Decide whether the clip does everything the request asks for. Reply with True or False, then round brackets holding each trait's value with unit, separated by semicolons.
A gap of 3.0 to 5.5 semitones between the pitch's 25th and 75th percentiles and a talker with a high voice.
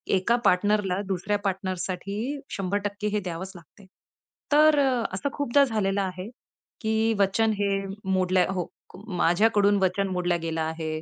False (2.6 semitones; 195 Hz)